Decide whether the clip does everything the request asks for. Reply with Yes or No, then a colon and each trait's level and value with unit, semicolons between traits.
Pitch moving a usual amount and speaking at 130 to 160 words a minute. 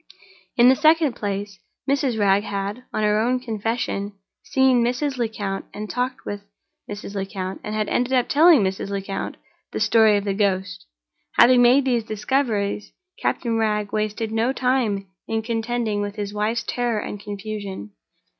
Yes: average, 3.2 semitones; average, 155 wpm